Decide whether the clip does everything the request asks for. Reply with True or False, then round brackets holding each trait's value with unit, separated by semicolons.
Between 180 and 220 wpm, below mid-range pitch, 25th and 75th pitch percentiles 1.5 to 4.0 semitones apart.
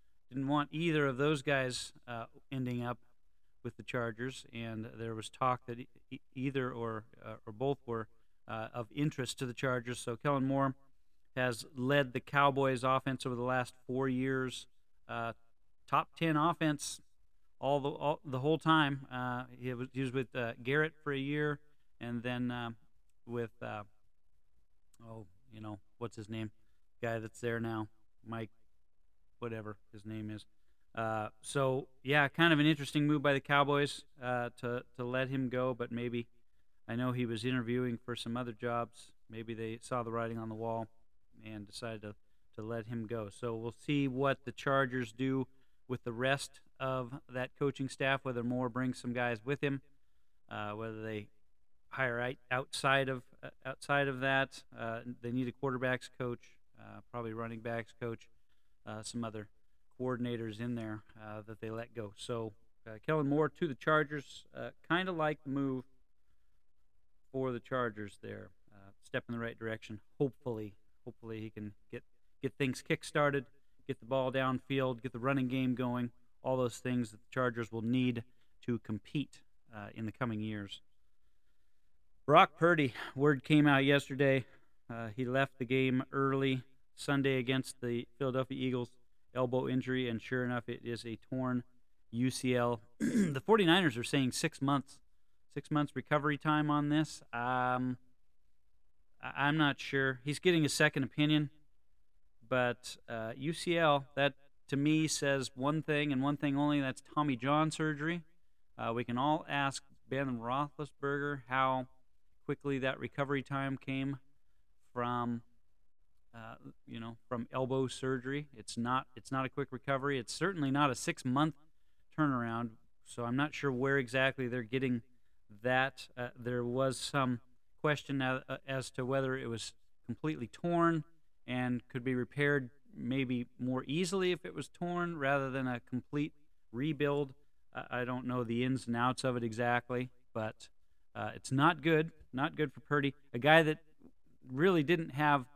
False (165 wpm; 125 Hz; 3.2 semitones)